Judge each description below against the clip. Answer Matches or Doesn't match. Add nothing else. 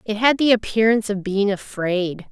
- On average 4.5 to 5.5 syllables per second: Matches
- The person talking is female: Matches